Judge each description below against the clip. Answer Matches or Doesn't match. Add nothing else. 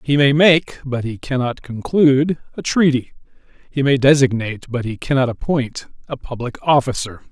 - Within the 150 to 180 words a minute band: Matches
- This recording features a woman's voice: Doesn't match